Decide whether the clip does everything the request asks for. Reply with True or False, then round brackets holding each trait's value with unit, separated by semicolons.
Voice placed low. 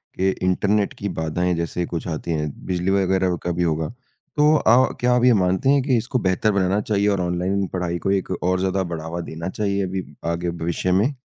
True (95 Hz)